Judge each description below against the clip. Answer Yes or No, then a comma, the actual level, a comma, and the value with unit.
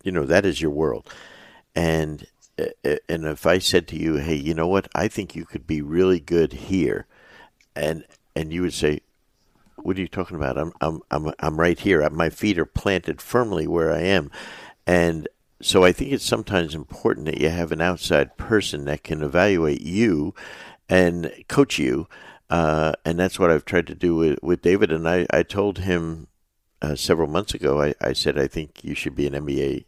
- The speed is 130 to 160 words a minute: No, average, 200 wpm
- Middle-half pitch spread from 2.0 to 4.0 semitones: Yes, average, 2.7 semitones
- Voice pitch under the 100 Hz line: Yes, very low, 85 Hz